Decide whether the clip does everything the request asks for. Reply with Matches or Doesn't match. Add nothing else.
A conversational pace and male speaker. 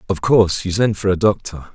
Doesn't match